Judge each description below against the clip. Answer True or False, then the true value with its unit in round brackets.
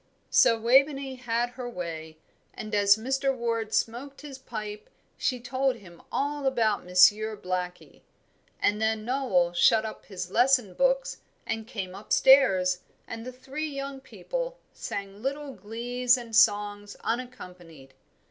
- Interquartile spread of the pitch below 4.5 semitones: False (4.8 semitones)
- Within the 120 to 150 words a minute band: True (140 wpm)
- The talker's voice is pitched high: True (230 Hz)